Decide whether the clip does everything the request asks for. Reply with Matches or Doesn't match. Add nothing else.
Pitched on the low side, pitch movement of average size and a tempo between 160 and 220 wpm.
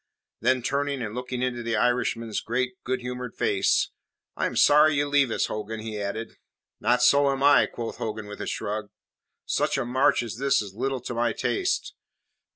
Matches